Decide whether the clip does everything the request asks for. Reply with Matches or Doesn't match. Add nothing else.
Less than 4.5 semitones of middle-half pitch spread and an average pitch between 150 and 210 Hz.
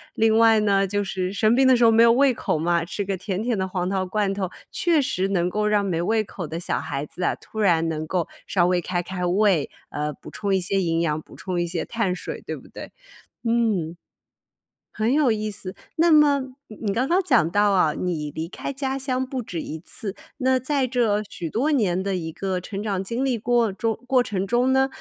Doesn't match